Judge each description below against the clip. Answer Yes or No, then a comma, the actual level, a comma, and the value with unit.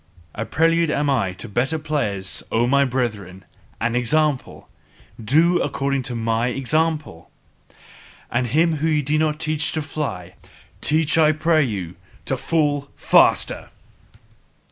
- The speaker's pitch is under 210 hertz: Yes, medium, 140 Hz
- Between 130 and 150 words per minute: Yes, slow, 135 wpm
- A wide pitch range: No, average, 4.9 semitones